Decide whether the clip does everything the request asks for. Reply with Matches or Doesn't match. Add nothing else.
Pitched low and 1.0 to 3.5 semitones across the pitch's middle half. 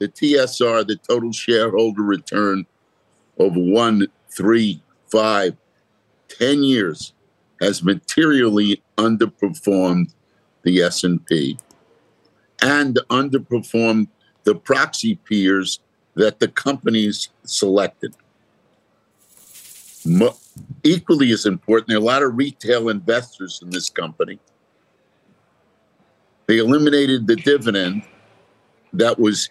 Matches